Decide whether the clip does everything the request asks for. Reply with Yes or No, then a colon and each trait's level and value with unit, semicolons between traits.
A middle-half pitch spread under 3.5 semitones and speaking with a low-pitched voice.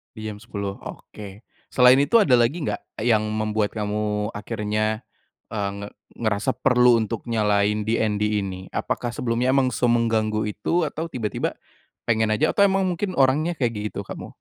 Yes: average, 3.1 semitones; low, 110 Hz